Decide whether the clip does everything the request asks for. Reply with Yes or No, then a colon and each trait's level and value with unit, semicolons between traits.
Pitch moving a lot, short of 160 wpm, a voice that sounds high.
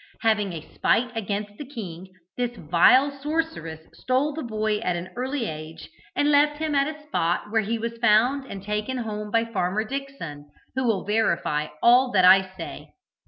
No: wide, 5.7 semitones; average, 175 wpm; high, 225 Hz